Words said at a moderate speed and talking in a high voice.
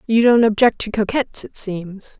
Yes: average, 190 wpm; high, 215 Hz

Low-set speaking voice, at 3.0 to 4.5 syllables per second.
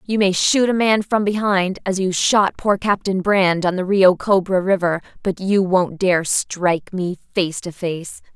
No: high, 190 Hz; 4.0 syllables/s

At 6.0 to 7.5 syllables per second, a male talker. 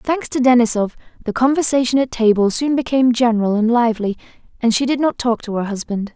No: 6.2 syllables/s; female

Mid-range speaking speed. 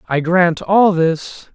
Yes: average, 155 wpm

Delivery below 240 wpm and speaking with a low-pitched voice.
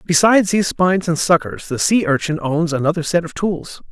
No: average, 200 wpm; medium, 170 Hz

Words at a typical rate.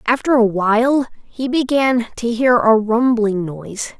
Yes: average, 150 wpm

